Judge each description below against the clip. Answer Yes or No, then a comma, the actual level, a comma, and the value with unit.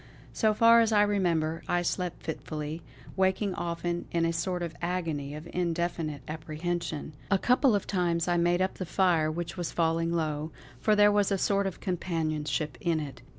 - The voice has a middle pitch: Yes, medium, 170 Hz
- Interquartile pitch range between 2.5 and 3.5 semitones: Yes, average, 2.9 semitones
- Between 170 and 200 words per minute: Yes, average, 180 wpm